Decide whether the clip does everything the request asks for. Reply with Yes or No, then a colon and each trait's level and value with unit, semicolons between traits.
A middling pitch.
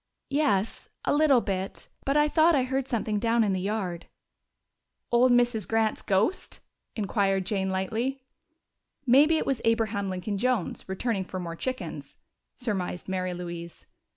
No: high, 220 Hz